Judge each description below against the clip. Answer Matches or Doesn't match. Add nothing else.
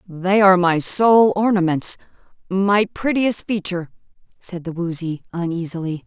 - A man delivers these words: Doesn't match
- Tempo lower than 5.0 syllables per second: Matches